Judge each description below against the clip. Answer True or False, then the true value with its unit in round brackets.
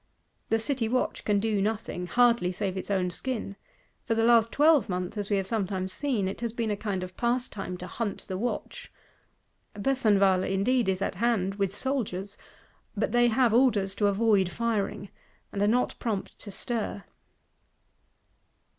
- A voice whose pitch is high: True (210 Hz)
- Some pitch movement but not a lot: True (3.5 semitones)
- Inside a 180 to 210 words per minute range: False (165 wpm)